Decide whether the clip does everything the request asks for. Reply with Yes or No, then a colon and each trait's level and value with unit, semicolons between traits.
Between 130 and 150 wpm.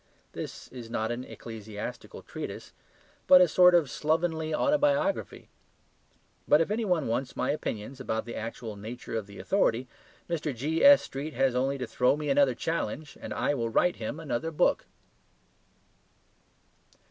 Yes: average, 145 wpm